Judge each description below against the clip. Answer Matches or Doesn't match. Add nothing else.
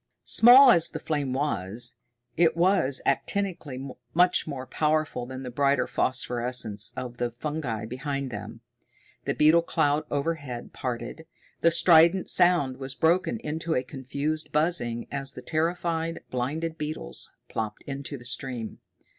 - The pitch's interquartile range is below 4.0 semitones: Doesn't match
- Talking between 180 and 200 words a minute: Doesn't match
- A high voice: Doesn't match